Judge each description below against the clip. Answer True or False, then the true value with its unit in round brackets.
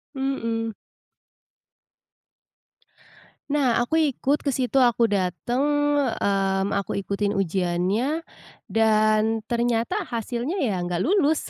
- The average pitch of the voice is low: False (230 Hz)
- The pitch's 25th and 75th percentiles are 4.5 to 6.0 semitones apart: True (5.0 semitones)